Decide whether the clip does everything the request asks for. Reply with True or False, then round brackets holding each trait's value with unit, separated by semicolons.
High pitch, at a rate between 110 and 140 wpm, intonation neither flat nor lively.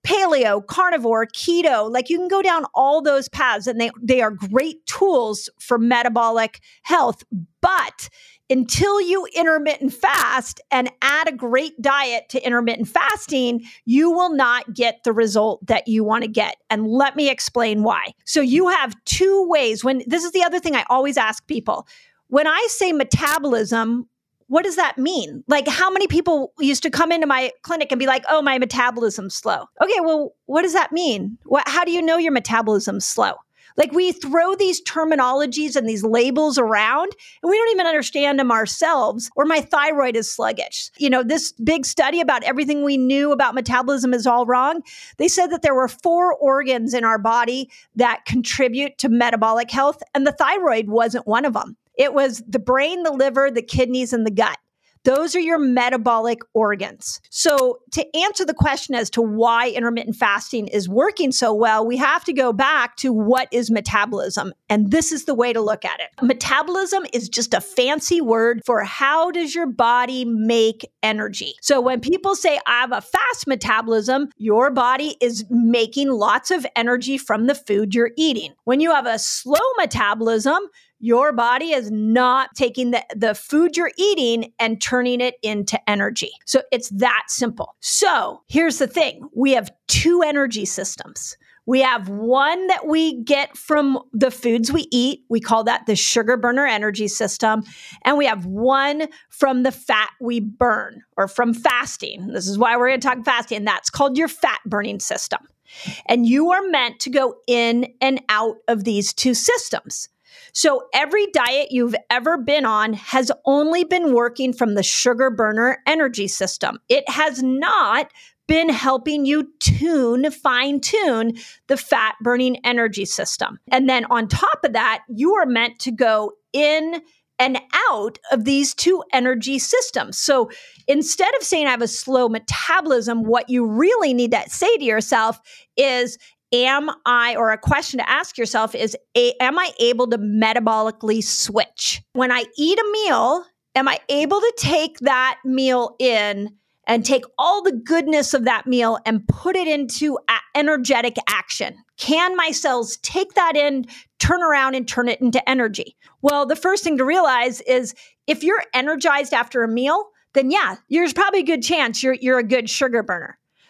False (260 Hz; 175 wpm; 4.8 semitones)